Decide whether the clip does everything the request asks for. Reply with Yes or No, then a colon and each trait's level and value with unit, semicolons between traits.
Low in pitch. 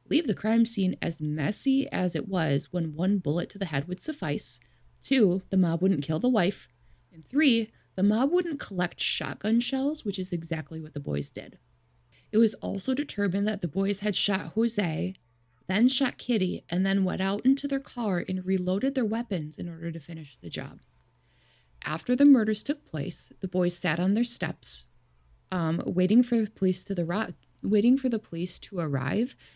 No: high, 190 Hz